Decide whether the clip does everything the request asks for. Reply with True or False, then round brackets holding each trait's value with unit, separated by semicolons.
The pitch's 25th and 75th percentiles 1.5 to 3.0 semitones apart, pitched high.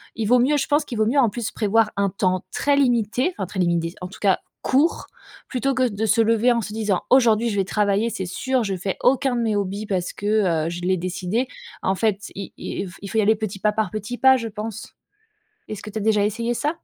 False (3.5 semitones; 215 Hz)